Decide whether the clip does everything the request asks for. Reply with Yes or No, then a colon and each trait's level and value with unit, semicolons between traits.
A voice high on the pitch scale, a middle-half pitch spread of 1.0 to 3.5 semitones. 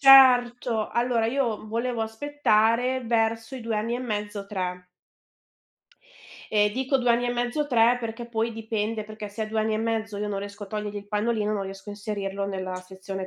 Yes: high, 220 Hz; narrow, 2.5 semitones